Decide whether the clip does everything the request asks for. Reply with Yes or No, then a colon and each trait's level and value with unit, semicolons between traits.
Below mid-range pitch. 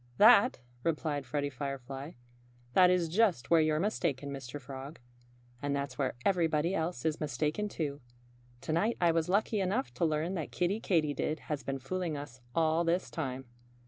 No: medium, 155 Hz